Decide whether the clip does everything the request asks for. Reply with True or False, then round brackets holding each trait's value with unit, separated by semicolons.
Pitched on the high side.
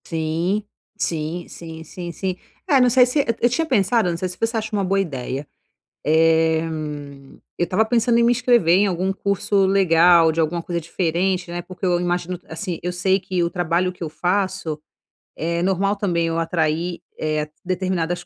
False (180 Hz)